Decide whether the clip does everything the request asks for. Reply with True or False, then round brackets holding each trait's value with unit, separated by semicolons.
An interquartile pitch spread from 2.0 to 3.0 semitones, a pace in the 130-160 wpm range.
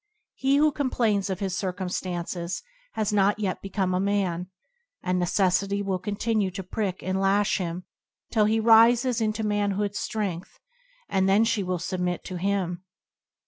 True (2.6 semitones; 155 wpm)